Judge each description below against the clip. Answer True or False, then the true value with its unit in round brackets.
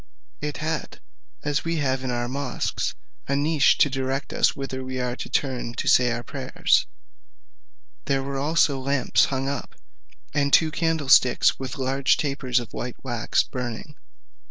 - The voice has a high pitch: False (135 Hz)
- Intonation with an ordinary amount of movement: False (2.1 semitones)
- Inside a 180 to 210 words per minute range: False (155 wpm)